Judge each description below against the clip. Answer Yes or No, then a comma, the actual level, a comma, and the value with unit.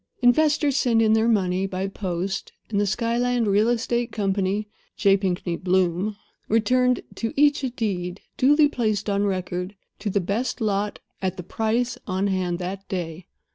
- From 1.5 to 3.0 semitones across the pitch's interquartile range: No, average, 3.9 semitones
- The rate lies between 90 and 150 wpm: No, average, 160 wpm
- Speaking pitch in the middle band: No, high, 205 Hz